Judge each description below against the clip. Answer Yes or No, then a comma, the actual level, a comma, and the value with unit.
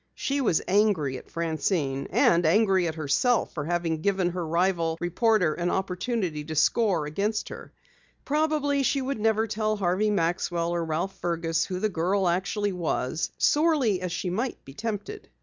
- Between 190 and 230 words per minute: No, average, 165 wpm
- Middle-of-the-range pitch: Yes, medium, 180 Hz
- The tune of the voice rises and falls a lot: No, average, 4.5 semitones